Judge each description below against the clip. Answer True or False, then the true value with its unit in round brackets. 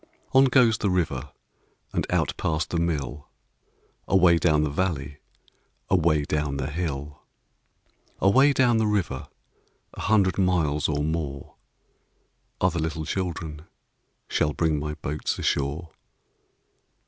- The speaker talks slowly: True (120 wpm)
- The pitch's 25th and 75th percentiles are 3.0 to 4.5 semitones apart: True (3.9 semitones)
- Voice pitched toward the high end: False (80 Hz)